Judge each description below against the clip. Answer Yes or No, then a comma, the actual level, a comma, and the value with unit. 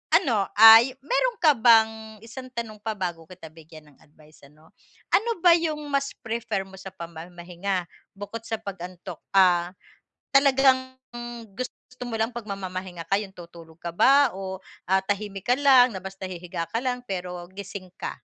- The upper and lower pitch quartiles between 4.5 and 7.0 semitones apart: Yes, average, 5.2 semitones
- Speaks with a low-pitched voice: No, high, 200 Hz